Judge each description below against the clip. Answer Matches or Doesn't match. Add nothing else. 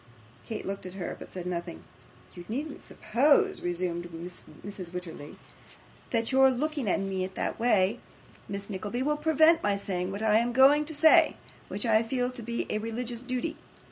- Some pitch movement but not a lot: Doesn't match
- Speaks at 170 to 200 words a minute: Matches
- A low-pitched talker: Doesn't match